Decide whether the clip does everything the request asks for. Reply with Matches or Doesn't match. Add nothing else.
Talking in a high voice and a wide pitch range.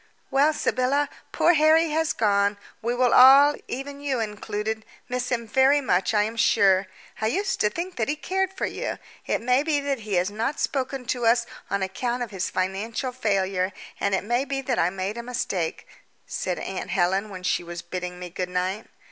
Matches